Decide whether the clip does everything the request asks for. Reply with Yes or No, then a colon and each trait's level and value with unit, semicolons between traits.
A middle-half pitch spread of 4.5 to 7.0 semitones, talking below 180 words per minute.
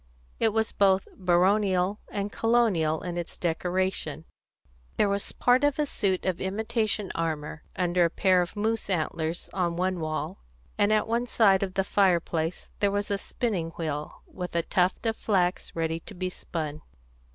No: average, 3.3 semitones; average, 165 wpm